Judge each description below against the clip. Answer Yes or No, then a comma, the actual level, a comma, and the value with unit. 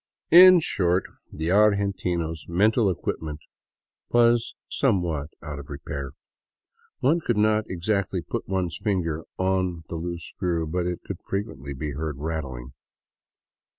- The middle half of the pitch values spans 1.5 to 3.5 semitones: No, average, 4.4 semitones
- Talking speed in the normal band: No, slow, 130 wpm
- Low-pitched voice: Yes, very low, 90 Hz